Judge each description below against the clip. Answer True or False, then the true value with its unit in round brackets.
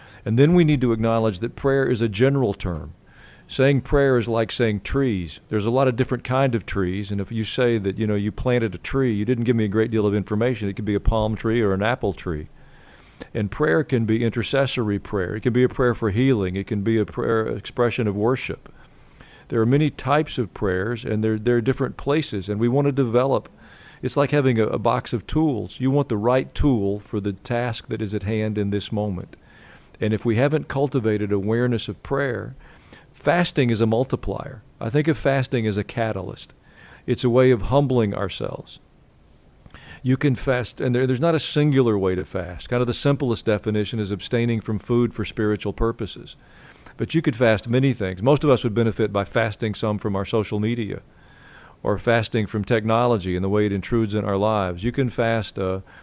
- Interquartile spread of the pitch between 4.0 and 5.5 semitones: False (3.6 semitones)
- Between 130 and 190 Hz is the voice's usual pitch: False (115 Hz)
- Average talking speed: False (215 wpm)